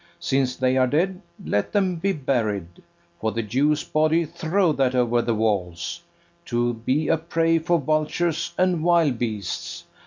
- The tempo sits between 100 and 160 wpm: Yes, average, 155 wpm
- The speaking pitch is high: No, medium, 140 Hz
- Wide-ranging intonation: Yes, wide, 5.9 semitones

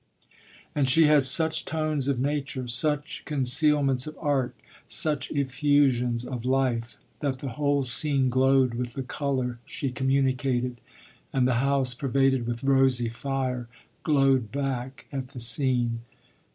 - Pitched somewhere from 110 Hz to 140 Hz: Yes, low, 135 Hz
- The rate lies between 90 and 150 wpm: Yes, slow, 135 wpm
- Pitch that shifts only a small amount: Yes, narrow, 2.2 semitones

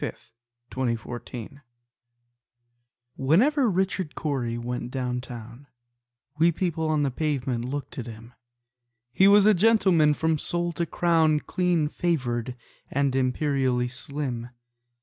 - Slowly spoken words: Yes, slow, 115 wpm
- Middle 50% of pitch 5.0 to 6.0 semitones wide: Yes, wide, 5.5 semitones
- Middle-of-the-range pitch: Yes, medium, 145 Hz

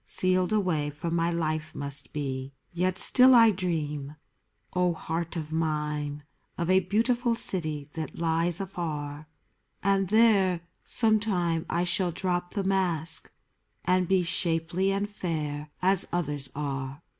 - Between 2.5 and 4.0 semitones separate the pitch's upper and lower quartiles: Yes, average, 3.7 semitones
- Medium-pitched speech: Yes, medium, 170 Hz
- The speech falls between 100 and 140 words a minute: Yes, slow, 135 wpm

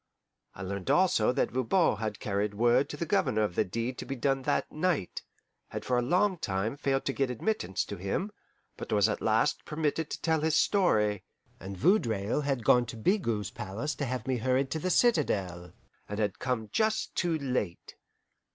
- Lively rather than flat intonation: Yes, wide, 6.6 semitones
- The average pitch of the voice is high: No, low, 125 Hz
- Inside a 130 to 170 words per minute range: No, average, 190 wpm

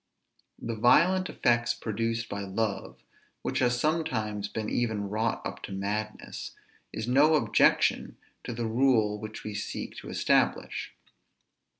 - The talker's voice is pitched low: Yes, low, 110 Hz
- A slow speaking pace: Yes, slow, 130 wpm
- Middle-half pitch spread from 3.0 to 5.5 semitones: No, narrow, 2.6 semitones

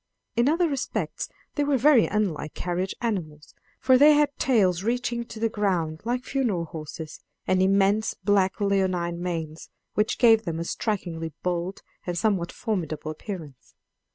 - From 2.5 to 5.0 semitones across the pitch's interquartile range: No, wide, 5.4 semitones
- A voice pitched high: Yes, high, 195 Hz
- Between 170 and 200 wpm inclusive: No, average, 150 wpm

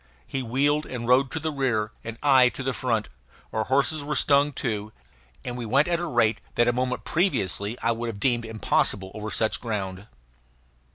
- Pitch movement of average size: Yes, average, 3.9 semitones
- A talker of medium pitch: No, low, 125 Hz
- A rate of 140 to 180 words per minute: No, average, 190 wpm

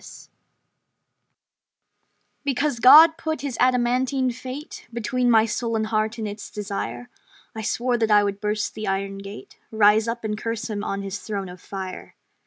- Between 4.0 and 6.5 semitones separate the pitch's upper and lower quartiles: No, average, 3.4 semitones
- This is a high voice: Yes, high, 220 Hz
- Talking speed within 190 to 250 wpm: No, average, 160 wpm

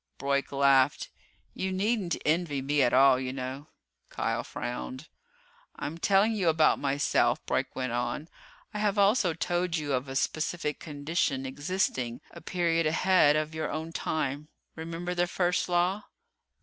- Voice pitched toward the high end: No, medium, 155 Hz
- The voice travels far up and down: No, average, 4.3 semitones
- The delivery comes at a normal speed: Yes, average, 150 wpm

